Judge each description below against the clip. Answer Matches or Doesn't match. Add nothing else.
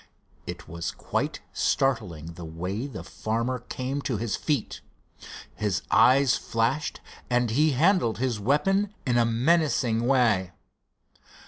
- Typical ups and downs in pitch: Matches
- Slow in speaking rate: Matches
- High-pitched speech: Doesn't match